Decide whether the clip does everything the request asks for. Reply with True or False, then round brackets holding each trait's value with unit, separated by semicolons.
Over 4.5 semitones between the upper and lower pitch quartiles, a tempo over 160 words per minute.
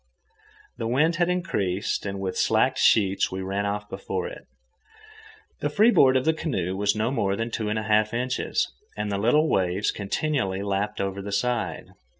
True (4.9 semitones; 175 wpm)